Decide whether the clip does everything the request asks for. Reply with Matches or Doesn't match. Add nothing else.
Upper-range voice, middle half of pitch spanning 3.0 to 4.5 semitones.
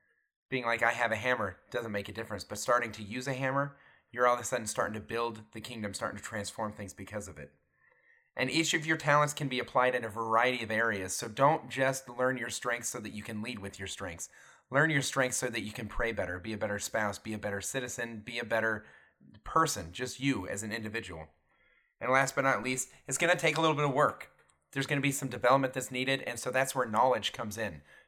Doesn't match